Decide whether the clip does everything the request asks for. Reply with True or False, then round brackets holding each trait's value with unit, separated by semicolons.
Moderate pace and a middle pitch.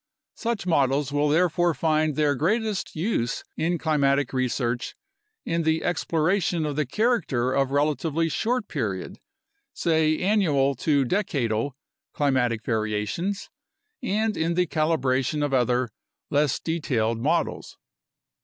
False (115 wpm; 150 Hz)